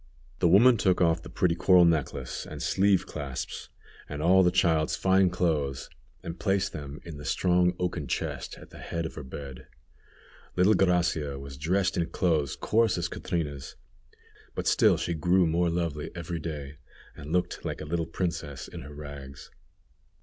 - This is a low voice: Yes, very low, 85 Hz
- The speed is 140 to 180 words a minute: Yes, average, 170 wpm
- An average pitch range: Yes, average, 3.5 semitones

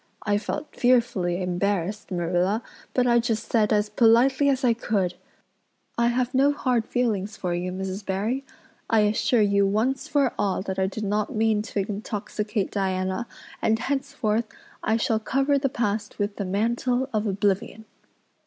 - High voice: Yes, high, 215 Hz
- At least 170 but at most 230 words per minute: No, average, 160 wpm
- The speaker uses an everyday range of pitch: Yes, average, 3.3 semitones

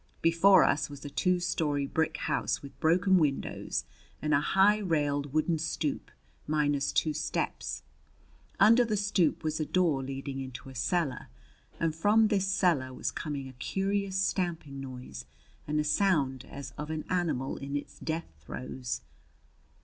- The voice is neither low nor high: Yes, medium, 155 Hz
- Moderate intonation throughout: Yes, average, 4.7 semitones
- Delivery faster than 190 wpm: No, average, 155 wpm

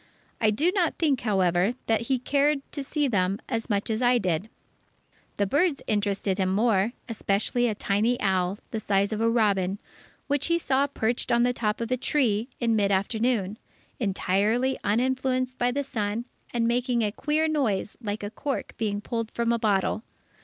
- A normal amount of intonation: Yes, average, 3.8 semitones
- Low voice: No, high, 230 Hz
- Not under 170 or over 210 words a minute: Yes, average, 180 wpm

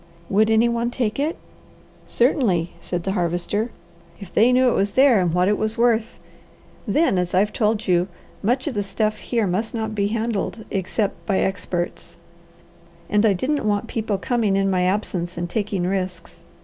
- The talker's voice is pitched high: Yes, high, 210 Hz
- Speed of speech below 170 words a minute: No, average, 175 wpm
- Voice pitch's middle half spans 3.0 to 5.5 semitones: Yes, average, 3.5 semitones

